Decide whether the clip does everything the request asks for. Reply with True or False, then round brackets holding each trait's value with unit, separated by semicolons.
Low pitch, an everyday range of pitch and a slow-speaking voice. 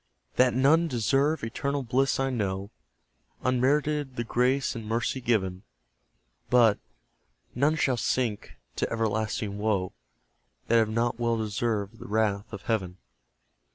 True (115 Hz; 3.3 semitones; 125 wpm)